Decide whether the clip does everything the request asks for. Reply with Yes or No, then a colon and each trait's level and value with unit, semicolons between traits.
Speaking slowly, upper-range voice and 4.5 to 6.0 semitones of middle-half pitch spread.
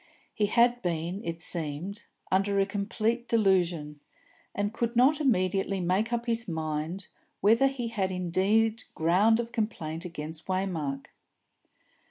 Yes: slow, 130 wpm; high, 195 Hz; average, 5.0 semitones